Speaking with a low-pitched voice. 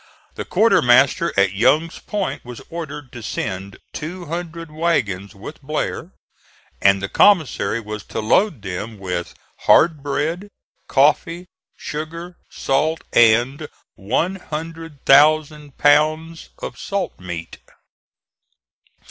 No: medium, 150 Hz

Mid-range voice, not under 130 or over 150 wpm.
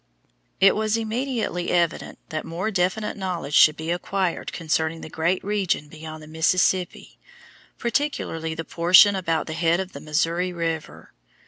Yes: medium, 175 Hz; average, 145 wpm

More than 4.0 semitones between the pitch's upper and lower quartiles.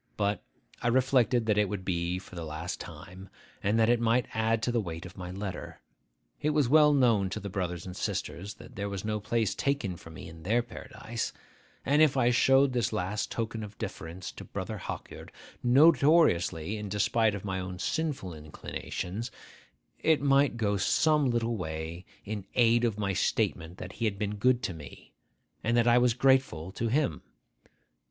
Yes: average, 4.8 semitones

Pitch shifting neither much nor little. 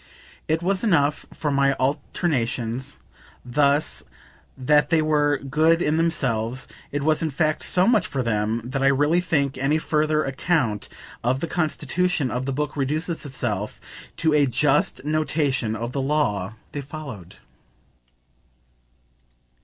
Yes: average, 3.2 semitones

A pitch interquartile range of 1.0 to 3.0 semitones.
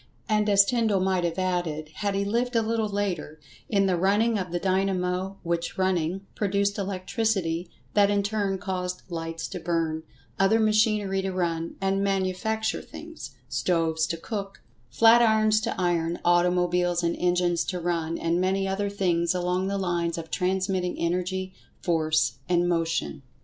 Yes: narrow, 2.6 semitones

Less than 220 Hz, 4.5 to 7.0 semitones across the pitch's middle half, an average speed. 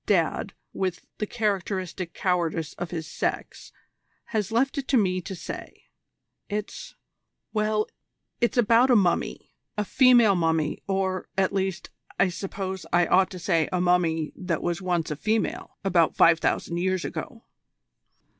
No: medium, 185 Hz; average, 3.5 semitones; average, 145 wpm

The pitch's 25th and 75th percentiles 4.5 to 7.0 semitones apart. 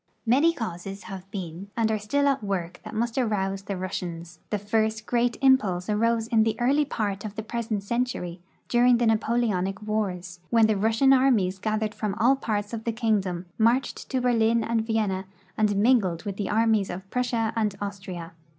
No: average, 3.2 semitones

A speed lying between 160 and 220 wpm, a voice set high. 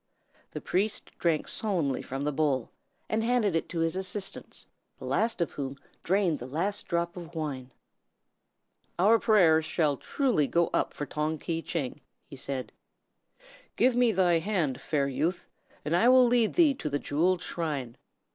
No: average, 165 wpm; medium, 170 Hz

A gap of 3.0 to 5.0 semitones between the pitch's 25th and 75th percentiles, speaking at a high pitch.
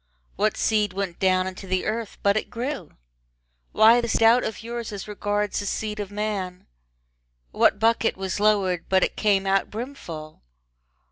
No: narrow, 2.6 semitones; high, 205 Hz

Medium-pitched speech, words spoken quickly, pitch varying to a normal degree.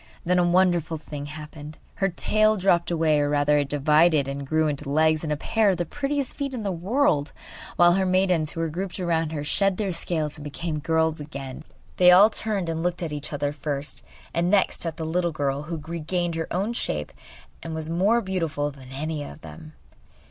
Yes: medium, 165 Hz; fast, 215 wpm; average, 3.3 semitones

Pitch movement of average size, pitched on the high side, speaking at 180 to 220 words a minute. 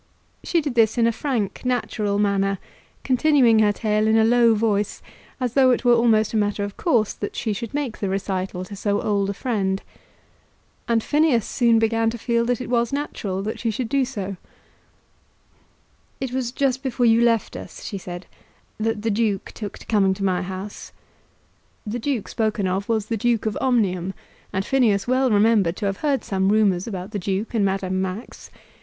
Yes: average, 3.3 semitones; high, 220 Hz; average, 190 wpm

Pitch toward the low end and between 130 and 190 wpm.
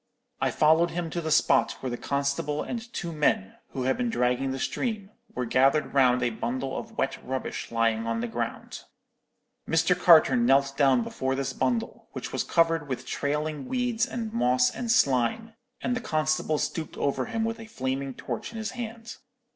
No: medium, 150 Hz; average, 185 wpm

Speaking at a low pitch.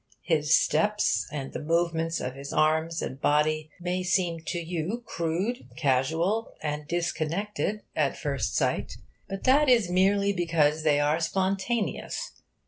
No: medium, 165 Hz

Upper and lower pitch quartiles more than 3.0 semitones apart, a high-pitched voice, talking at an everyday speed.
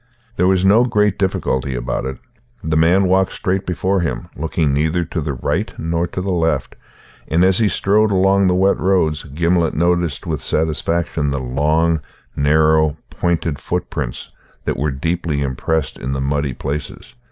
No: average, 4.0 semitones; very low, 80 Hz; average, 165 wpm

